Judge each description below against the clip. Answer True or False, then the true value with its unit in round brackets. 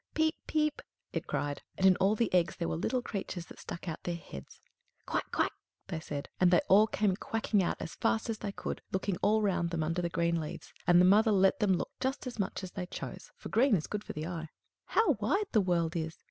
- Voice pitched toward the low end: False (190 Hz)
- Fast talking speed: True (235 wpm)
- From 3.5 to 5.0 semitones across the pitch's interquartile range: True (4.1 semitones)